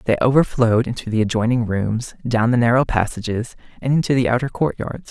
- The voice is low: Yes, low, 120 Hz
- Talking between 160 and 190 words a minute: Yes, average, 165 wpm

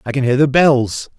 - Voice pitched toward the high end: No, low, 135 Hz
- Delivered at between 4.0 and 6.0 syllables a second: Yes, 4.9 syllables/s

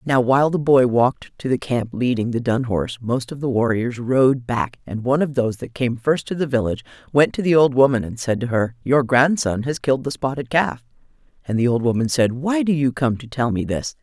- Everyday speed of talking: No, fast, 245 wpm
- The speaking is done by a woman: Yes, female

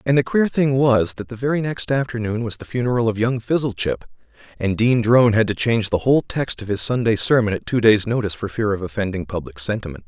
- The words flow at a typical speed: No, fast, 230 wpm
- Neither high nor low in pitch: No, low, 115 Hz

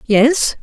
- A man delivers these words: No, female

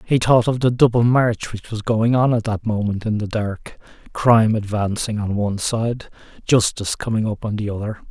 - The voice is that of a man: Yes, male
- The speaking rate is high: No, average, 195 wpm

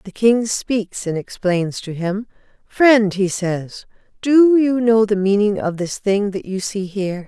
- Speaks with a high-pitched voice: Yes, high, 205 Hz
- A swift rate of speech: No, average, 180 wpm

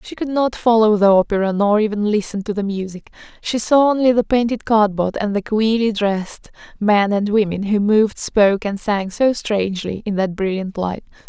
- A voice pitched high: Yes, high, 210 Hz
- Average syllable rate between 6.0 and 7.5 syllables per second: No, 5.1 syllables/s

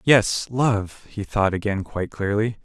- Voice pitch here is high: No, low, 105 Hz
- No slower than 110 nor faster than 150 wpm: Yes, slow, 135 wpm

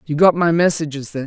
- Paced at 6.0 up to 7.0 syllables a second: Yes, 6.1 syllables/s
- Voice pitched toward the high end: No, medium, 155 Hz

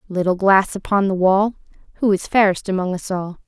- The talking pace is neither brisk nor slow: Yes, average, 190 wpm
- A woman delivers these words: Yes, female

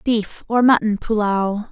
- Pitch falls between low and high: No, high, 220 Hz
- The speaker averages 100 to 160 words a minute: Yes, average, 140 wpm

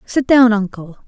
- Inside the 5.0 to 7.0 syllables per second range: No, 4.5 syllables/s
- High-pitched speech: Yes, high, 220 Hz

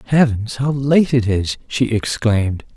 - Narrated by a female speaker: No, male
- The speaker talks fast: No, average, 150 wpm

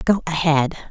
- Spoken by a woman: Yes, female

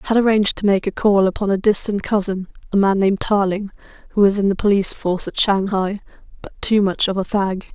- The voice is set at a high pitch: Yes, high, 200 Hz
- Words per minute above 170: Yes, average, 200 wpm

